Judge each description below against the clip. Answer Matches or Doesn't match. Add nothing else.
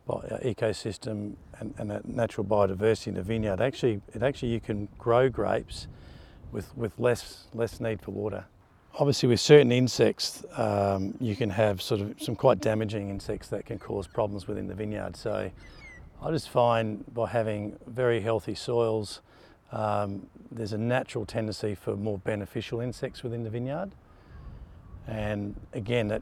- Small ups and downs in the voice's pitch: Matches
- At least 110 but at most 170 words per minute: Matches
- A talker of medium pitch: Doesn't match